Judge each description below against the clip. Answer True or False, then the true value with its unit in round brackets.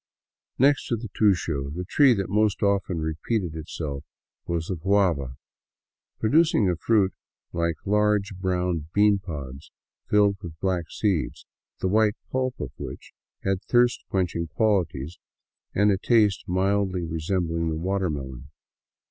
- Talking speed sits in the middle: False (130 wpm)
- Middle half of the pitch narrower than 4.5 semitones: True (4.1 semitones)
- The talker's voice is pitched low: True (95 Hz)